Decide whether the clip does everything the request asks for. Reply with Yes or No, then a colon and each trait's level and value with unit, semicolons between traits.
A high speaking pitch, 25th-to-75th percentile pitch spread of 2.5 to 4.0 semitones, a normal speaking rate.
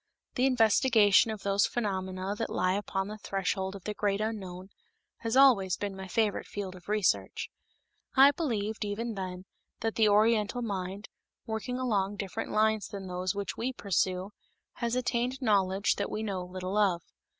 Yes: high, 205 Hz; average, 2.8 semitones; average, 160 wpm